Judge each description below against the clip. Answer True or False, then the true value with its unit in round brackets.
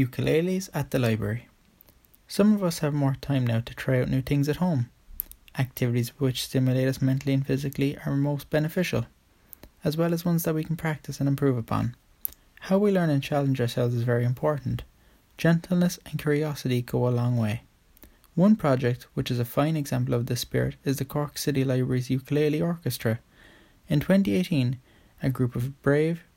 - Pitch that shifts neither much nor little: True (3.6 semitones)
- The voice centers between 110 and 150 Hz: True (135 Hz)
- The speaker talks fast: False (180 wpm)